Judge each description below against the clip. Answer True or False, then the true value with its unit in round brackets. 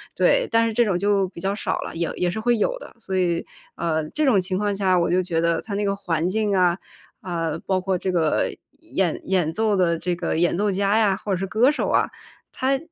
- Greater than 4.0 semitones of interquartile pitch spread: False (3.3 semitones)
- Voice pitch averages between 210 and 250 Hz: False (190 Hz)